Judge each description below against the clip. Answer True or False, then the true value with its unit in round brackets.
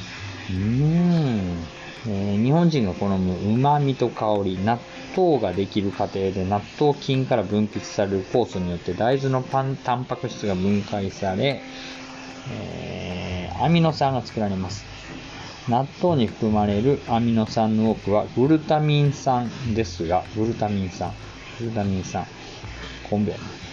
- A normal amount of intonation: True (4.8 semitones)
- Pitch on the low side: True (110 Hz)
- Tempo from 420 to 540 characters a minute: False (270 characters per minute)